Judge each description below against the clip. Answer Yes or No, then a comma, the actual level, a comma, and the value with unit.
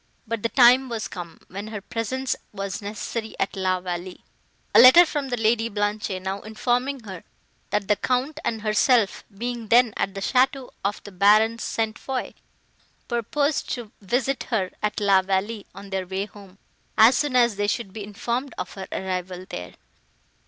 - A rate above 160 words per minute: Yes, average, 175 wpm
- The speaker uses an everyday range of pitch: Yes, average, 3.7 semitones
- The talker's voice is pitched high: Yes, high, 215 Hz